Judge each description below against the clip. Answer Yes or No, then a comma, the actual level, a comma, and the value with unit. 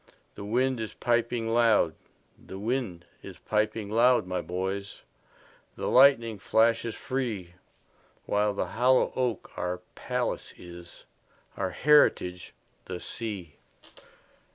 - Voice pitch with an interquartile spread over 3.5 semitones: Yes, average, 4.6 semitones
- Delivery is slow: Yes, slow, 95 wpm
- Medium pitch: No, low, 110 Hz